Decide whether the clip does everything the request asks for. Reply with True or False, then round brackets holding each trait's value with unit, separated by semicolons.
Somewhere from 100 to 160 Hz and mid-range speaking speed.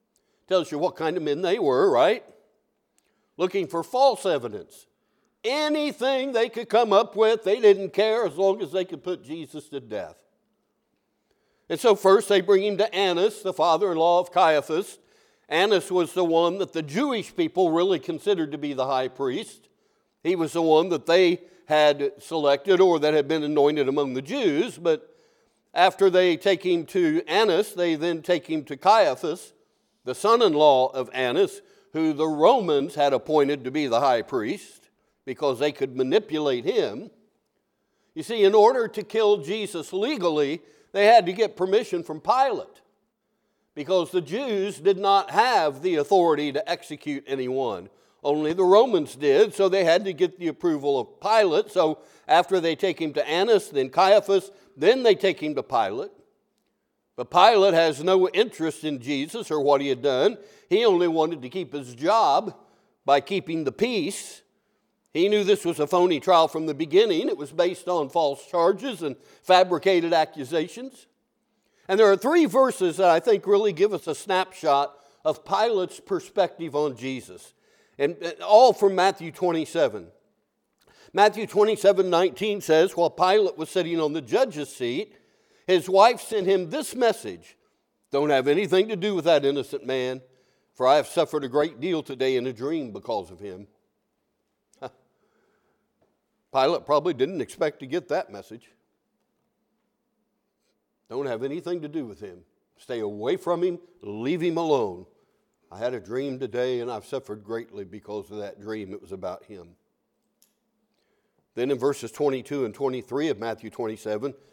False (180 Hz; 165 wpm)